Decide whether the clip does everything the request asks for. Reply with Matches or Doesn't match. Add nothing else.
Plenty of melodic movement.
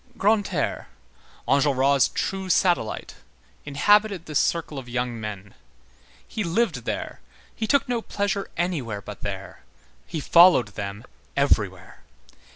Matches